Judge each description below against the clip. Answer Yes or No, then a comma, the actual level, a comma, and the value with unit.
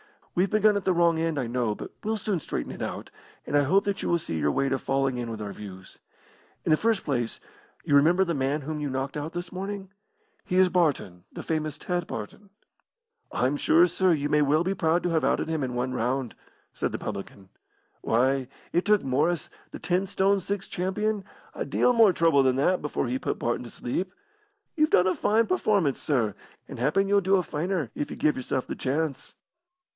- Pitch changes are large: Yes, wide, 6.0 semitones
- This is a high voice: No, medium, 155 Hz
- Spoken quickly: Yes, fast, 215 wpm